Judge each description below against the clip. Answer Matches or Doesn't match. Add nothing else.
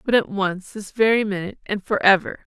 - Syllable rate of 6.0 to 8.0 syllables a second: Doesn't match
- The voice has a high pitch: Matches